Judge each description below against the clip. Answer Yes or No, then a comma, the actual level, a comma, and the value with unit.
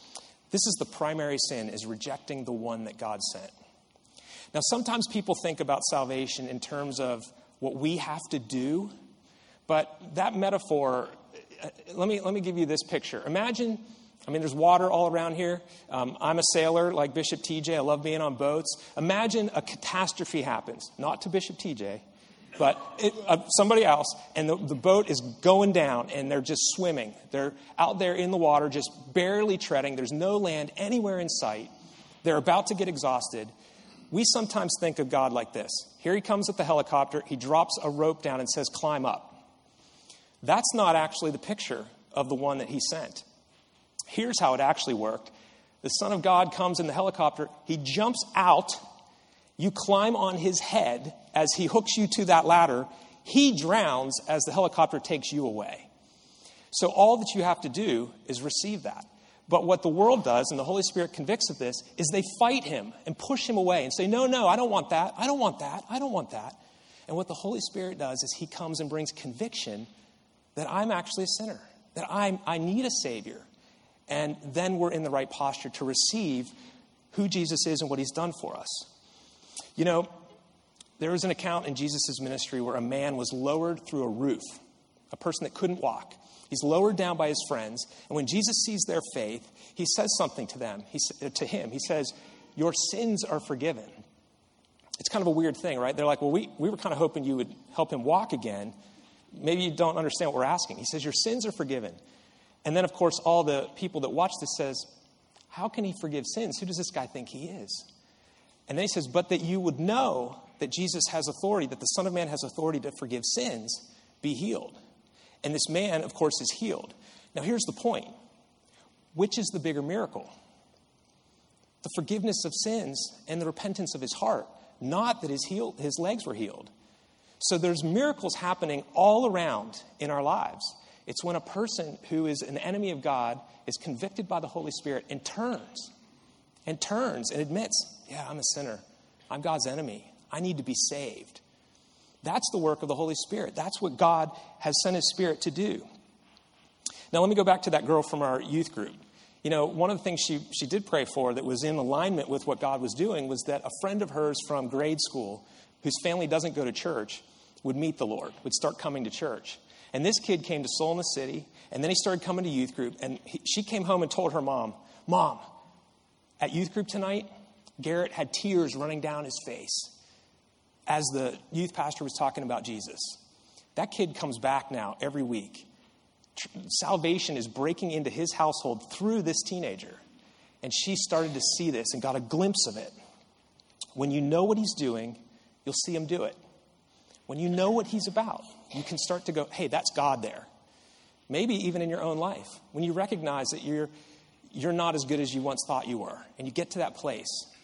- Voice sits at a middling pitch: Yes, medium, 165 Hz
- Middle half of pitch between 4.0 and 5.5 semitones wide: Yes, average, 4.9 semitones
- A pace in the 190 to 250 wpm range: Yes, average, 200 wpm